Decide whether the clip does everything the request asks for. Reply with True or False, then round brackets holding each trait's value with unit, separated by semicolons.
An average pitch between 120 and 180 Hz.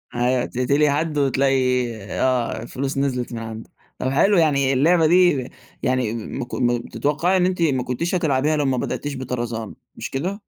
True (135 Hz)